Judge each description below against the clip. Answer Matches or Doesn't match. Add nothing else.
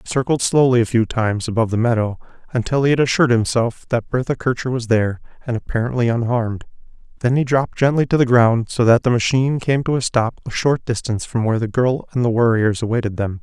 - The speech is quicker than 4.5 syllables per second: Matches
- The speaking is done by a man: Matches